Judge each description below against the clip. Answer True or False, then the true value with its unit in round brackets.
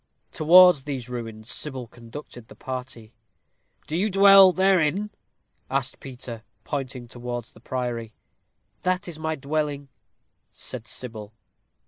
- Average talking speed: False (115 wpm)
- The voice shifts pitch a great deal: False (4.7 semitones)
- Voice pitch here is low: True (130 Hz)